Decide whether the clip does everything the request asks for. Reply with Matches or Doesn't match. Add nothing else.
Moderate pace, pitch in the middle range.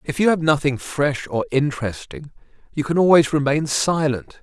Matches